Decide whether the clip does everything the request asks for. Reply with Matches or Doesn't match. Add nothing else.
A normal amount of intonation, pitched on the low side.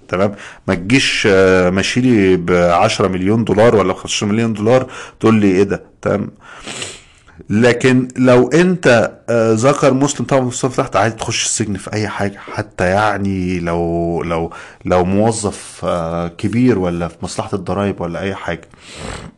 Matches